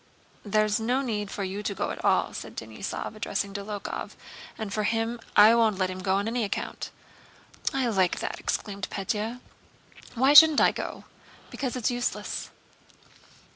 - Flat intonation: No, average, 3.1 semitones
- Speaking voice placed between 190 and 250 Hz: Yes, high, 215 Hz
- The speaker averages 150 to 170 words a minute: Yes, average, 165 wpm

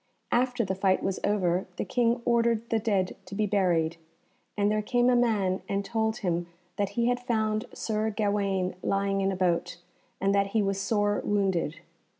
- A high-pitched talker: Yes, high, 205 Hz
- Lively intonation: No, narrow, 2.6 semitones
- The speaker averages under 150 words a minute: No, average, 180 wpm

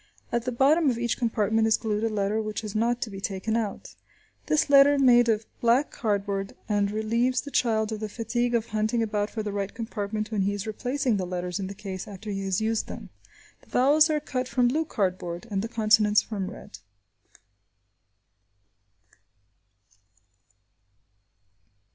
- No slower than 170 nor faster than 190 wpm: Yes, average, 175 wpm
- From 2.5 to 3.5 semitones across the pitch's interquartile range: Yes, average, 2.8 semitones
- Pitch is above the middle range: Yes, high, 220 Hz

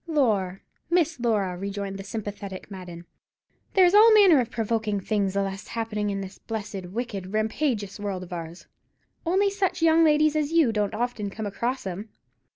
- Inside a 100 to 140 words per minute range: No, average, 160 wpm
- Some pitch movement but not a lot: No, wide, 6.7 semitones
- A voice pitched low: No, high, 215 Hz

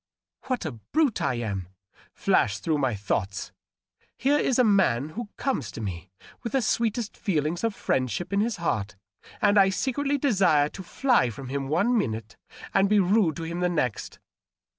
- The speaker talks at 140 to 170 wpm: No, average, 185 wpm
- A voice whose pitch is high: No, medium, 175 Hz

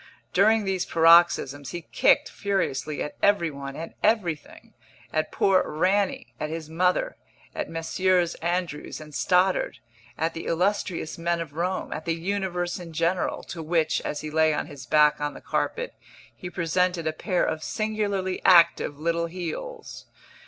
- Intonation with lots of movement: No, average, 2.9 semitones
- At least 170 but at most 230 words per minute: No, average, 155 wpm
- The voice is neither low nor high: Yes, medium, 170 Hz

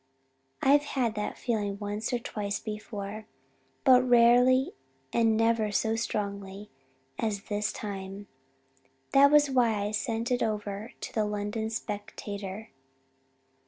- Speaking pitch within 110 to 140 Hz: No, high, 215 Hz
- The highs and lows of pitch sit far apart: No, narrow, 2.4 semitones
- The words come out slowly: Yes, slow, 125 wpm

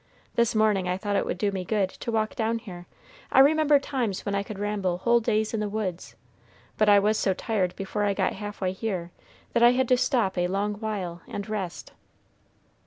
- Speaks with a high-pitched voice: Yes, high, 210 Hz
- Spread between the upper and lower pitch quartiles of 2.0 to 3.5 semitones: Yes, average, 2.8 semitones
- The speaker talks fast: Yes, fast, 215 wpm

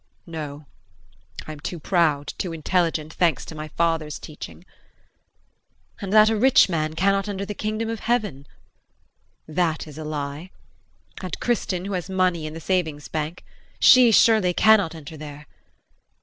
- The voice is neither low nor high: Yes, medium, 170 Hz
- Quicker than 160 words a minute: No, average, 150 wpm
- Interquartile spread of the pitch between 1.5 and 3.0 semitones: No, average, 4.3 semitones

